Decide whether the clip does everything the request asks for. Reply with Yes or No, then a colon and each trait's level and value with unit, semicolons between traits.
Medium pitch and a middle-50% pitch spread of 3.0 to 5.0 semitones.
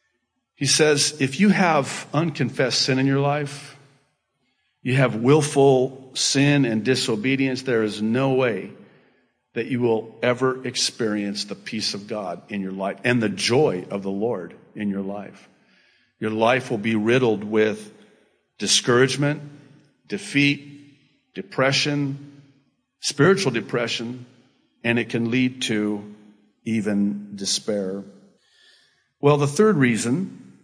No: low, 130 Hz; average, 4.4 semitones